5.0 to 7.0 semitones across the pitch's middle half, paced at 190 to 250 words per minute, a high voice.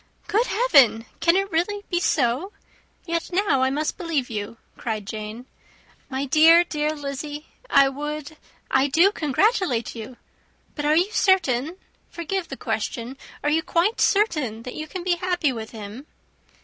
No: wide, 5.5 semitones; average, 155 wpm; very high, 300 Hz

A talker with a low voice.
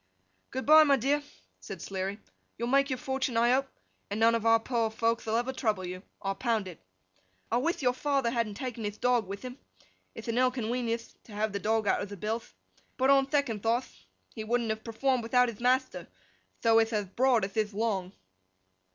No: high, 230 Hz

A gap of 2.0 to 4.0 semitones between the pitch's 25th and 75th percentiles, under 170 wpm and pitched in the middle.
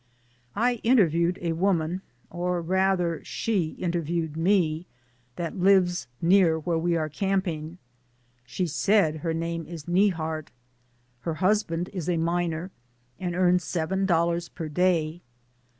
Yes: narrow, 2.4 semitones; average, 140 wpm; medium, 170 Hz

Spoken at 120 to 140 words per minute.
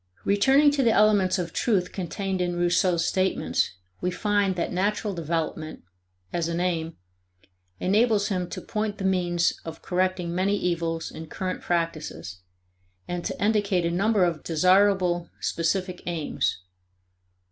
Yes: slow, 135 wpm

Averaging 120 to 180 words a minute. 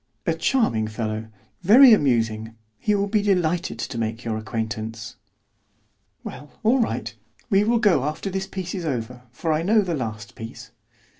Yes: average, 160 wpm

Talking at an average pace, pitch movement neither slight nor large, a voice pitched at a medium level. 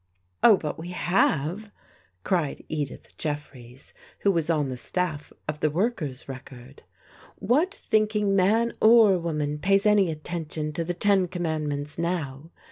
Yes: average, 145 wpm; average, 4.9 semitones; medium, 165 Hz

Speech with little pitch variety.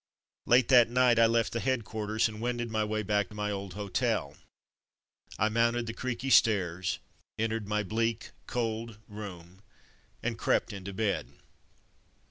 Yes: narrow, 2.3 semitones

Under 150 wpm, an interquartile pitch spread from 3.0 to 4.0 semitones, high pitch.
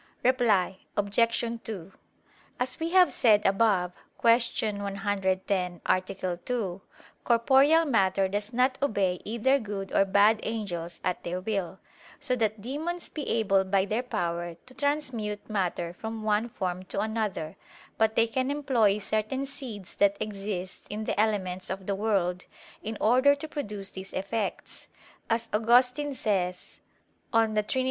Yes: average, 140 wpm; average, 3.7 semitones; high, 210 Hz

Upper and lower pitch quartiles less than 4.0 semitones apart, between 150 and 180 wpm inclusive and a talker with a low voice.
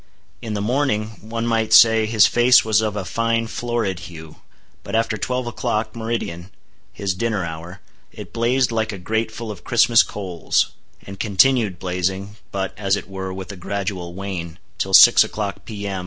Yes: average, 3.2 semitones; average, 155 wpm; low, 105 Hz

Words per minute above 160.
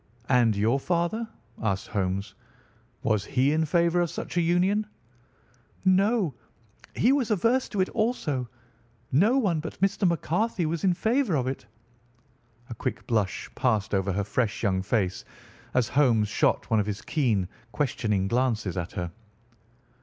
No: average, 150 wpm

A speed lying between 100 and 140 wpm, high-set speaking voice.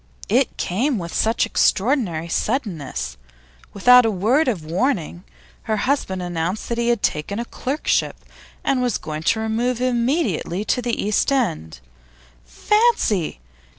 Yes: slow, 135 wpm; high, 220 Hz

